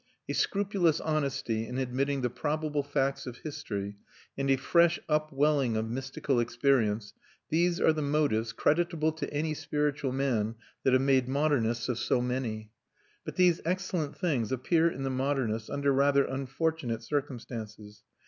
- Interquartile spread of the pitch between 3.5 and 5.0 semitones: Yes, average, 4.0 semitones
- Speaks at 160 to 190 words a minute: No, average, 150 wpm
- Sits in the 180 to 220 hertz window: No, low, 135 Hz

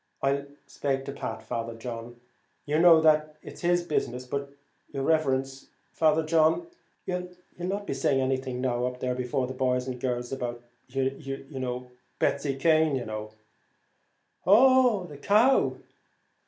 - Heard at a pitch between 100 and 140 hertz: Yes, low, 135 Hz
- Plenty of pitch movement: No, average, 4.0 semitones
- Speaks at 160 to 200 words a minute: No, average, 140 wpm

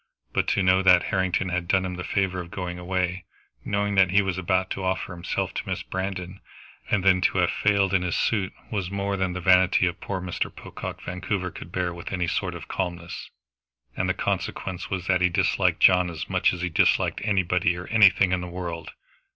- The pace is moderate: No, fast, 210 wpm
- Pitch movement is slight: Yes, narrow, 1.3 semitones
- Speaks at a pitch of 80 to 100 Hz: Yes, very low, 90 Hz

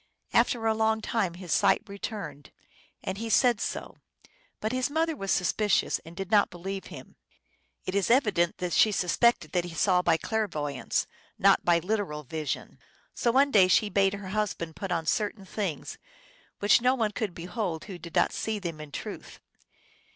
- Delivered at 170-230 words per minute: Yes, average, 180 wpm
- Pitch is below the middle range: No, high, 195 Hz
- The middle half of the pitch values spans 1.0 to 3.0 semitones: No, average, 4.2 semitones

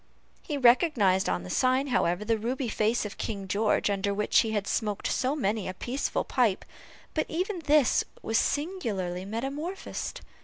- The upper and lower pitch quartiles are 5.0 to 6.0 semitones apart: Yes, wide, 5.6 semitones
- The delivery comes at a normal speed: Yes, average, 160 wpm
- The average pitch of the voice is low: No, high, 225 Hz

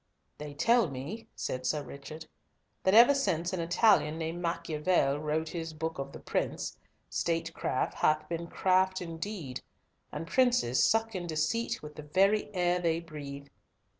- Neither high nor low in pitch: Yes, medium, 165 Hz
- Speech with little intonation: No, average, 3.7 semitones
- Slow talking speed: No, average, 150 wpm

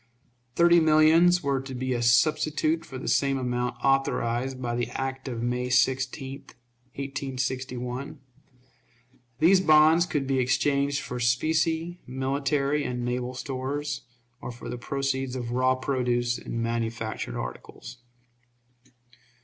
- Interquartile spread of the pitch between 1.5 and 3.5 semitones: Yes, average, 2.7 semitones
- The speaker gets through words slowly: Yes, slow, 125 wpm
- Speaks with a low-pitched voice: Yes, low, 130 Hz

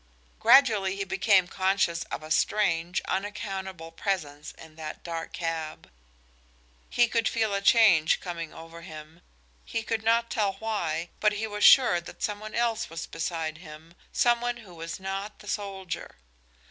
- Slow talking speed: No, average, 160 wpm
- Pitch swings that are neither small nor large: Yes, average, 4.4 semitones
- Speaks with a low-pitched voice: No, high, 190 Hz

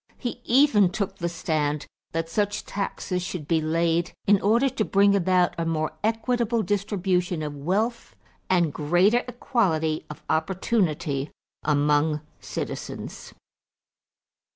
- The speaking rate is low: Yes, slow, 120 wpm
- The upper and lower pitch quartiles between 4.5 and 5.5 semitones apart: Yes, average, 4.8 semitones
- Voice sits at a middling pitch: Yes, medium, 180 Hz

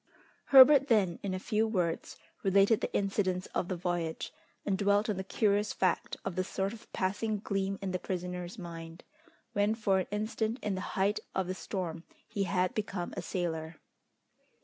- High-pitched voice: Yes, high, 195 Hz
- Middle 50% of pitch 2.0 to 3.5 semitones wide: Yes, narrow, 2.4 semitones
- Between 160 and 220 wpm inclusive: Yes, average, 175 wpm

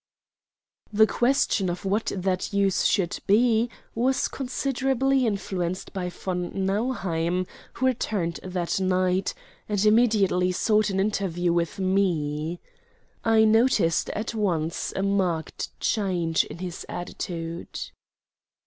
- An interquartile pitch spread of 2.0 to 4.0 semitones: Yes, average, 3.7 semitones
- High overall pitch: Yes, high, 195 Hz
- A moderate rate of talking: No, slow, 115 wpm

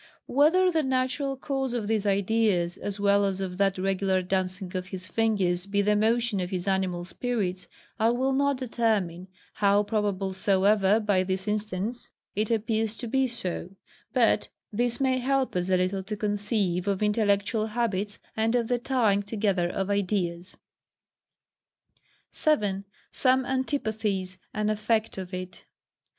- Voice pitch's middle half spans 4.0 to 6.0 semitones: No, average, 3.5 semitones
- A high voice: Yes, high, 205 Hz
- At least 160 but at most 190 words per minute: No, average, 150 wpm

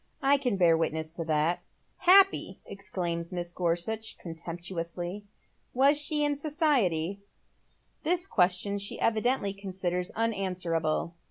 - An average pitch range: No, wide, 6.4 semitones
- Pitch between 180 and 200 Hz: Yes, high, 190 Hz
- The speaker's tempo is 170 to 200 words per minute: No, slow, 135 wpm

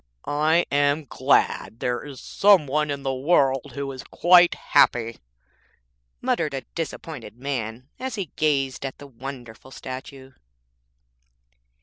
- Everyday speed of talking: No, slow, 125 wpm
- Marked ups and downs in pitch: No, average, 2.8 semitones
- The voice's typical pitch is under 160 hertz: Yes, medium, 140 Hz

